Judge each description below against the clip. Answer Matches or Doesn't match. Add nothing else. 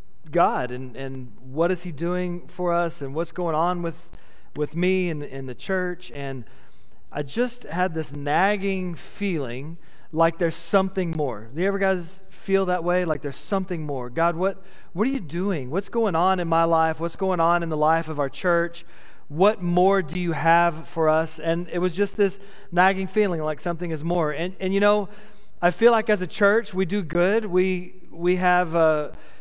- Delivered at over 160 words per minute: Matches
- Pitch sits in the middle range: Matches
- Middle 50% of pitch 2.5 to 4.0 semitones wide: Matches